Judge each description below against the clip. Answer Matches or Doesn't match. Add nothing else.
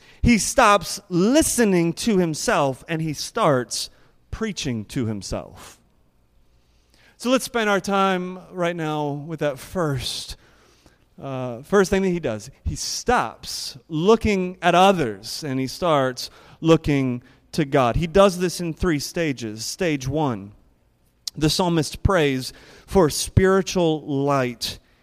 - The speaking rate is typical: Doesn't match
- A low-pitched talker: Doesn't match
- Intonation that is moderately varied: Doesn't match